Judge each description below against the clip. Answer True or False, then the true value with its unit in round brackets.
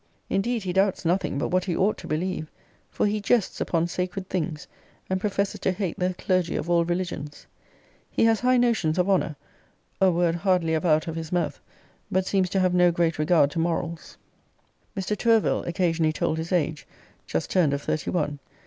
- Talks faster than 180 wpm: True (190 wpm)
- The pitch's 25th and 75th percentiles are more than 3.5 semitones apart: False (2.7 semitones)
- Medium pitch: True (180 Hz)